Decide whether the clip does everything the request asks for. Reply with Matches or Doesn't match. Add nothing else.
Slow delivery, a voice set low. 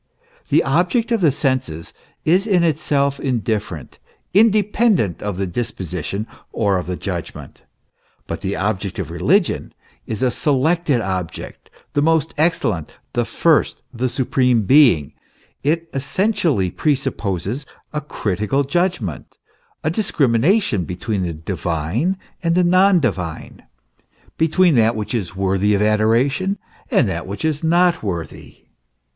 Matches